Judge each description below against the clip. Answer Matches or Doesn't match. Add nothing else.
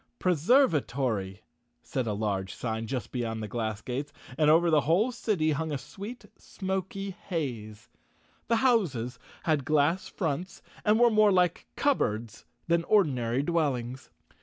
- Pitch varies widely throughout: Matches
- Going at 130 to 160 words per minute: Matches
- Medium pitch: Matches